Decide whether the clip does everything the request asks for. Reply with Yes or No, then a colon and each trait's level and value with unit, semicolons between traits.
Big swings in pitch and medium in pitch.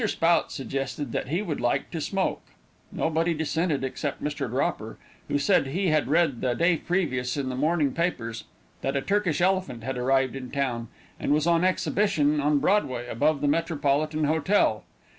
No: average, 4.0 semitones; medium, 150 Hz